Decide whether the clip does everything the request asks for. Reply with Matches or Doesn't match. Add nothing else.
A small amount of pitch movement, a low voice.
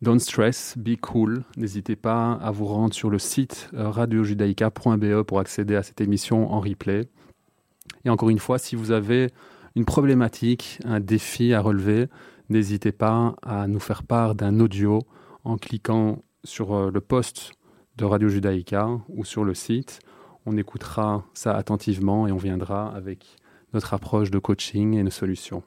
Matches